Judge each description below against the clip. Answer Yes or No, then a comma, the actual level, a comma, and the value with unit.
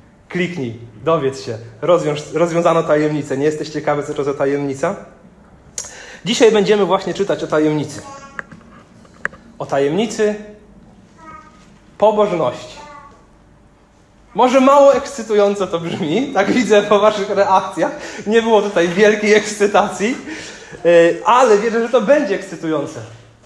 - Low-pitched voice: No, high, 195 Hz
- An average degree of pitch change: No, wide, 6.0 semitones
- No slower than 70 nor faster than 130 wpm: Yes, slow, 110 wpm